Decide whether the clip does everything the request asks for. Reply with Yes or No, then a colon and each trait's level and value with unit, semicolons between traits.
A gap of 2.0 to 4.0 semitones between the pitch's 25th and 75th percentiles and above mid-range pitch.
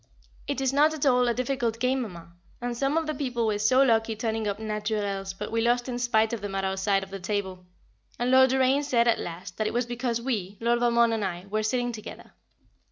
Yes: average, 3.5 semitones; high, 230 Hz